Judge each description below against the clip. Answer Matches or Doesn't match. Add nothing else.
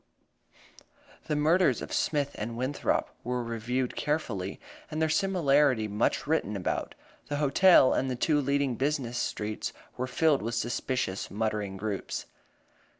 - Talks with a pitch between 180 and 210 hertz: Doesn't match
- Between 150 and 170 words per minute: Doesn't match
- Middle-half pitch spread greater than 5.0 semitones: Doesn't match